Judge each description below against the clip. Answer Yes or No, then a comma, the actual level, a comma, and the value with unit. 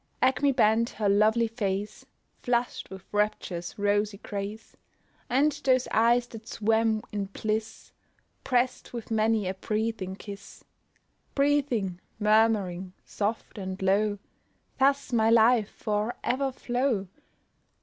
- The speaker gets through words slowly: Yes, slow, 115 wpm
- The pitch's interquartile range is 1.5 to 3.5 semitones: Yes, average, 2.8 semitones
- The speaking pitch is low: No, high, 220 Hz